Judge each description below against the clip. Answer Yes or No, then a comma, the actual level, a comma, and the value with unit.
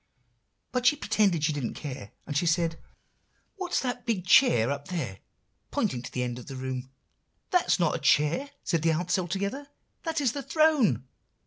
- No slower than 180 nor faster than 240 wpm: Yes, average, 195 wpm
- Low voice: No, medium, 175 Hz